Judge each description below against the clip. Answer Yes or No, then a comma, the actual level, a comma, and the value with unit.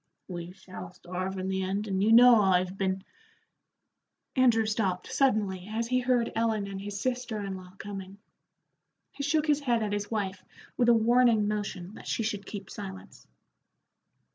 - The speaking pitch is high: Yes, high, 205 Hz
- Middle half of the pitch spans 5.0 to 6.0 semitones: No, average, 3.4 semitones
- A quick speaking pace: No, average, 170 wpm